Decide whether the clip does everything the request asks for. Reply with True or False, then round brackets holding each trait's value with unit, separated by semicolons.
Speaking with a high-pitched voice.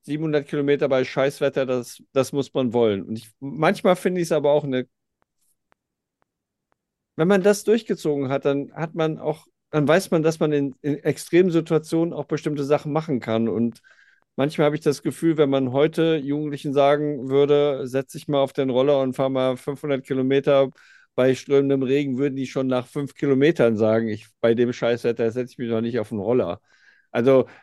False (140 Hz)